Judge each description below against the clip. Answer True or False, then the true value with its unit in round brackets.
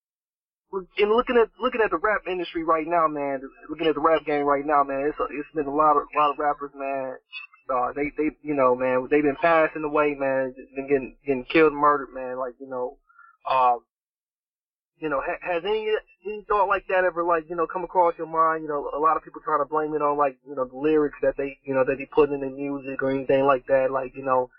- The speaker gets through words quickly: True (250 wpm)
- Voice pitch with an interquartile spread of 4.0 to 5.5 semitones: False (3.2 semitones)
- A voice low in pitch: False (145 Hz)